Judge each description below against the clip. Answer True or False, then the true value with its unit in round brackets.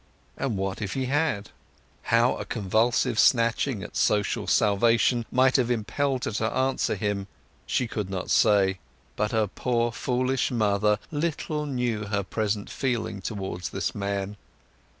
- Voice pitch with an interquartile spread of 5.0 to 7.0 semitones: False (3.7 semitones)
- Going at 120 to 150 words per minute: True (145 wpm)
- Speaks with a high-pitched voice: False (110 Hz)